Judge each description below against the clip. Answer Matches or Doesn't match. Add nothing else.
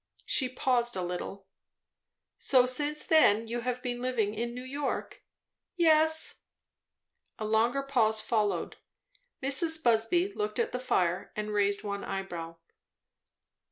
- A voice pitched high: Matches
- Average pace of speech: Doesn't match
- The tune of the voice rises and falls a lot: Doesn't match